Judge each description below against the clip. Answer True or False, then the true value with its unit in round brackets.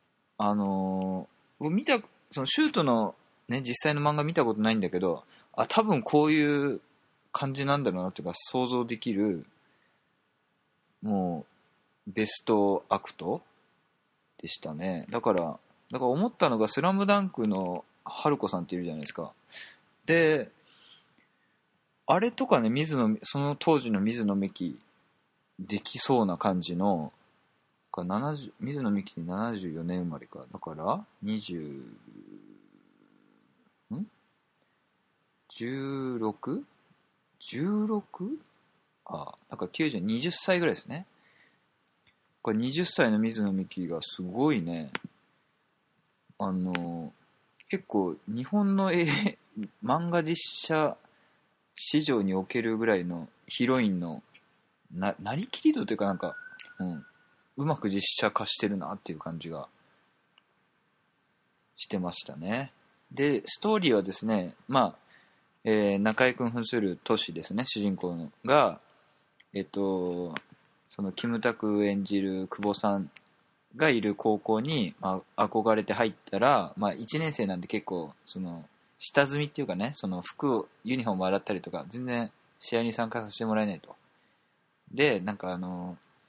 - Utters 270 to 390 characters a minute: False (240 characters per minute)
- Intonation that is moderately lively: False (7.9 semitones)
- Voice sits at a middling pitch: False (115 Hz)